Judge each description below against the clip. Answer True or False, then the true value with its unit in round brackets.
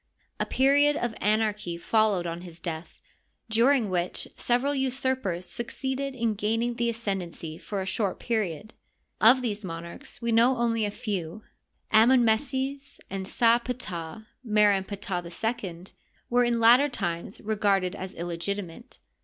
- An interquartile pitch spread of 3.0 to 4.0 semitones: False (4.6 semitones)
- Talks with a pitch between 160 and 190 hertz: False (220 Hz)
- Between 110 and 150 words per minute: True (140 wpm)